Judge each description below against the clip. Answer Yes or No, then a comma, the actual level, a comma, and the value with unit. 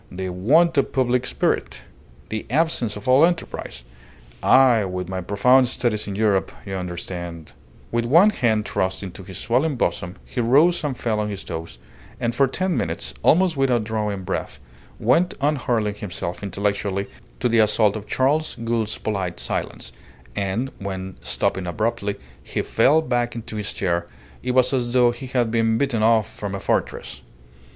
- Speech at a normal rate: Yes, average, 170 wpm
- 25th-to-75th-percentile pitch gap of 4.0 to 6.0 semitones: Yes, average, 4.6 semitones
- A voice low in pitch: Yes, low, 110 Hz